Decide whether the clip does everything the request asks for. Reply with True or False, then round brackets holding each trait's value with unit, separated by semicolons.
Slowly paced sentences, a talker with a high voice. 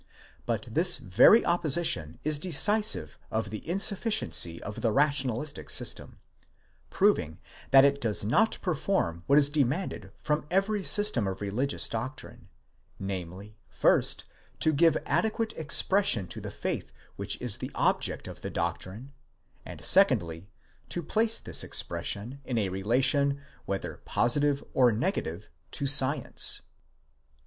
False (130 wpm; 135 Hz)